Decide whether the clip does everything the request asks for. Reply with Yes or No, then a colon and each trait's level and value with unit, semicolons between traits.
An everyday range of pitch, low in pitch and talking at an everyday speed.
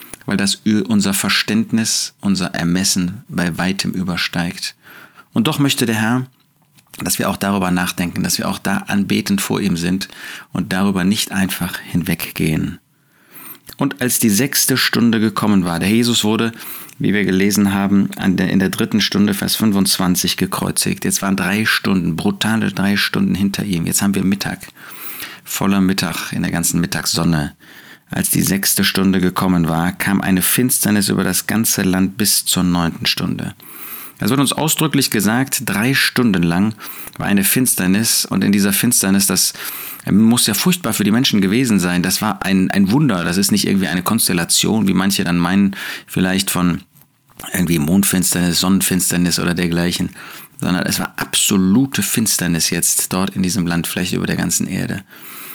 Yes: average, 3.8 semitones; low, 100 Hz; average, 160 wpm